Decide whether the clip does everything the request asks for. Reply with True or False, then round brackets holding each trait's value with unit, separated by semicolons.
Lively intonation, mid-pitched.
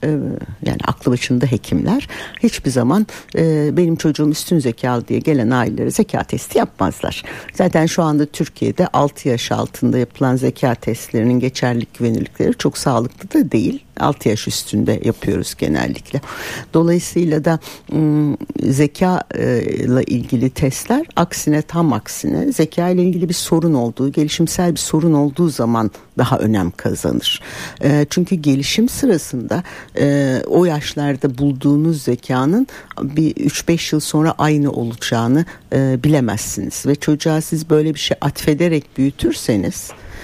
False (4.5 semitones; 145 Hz)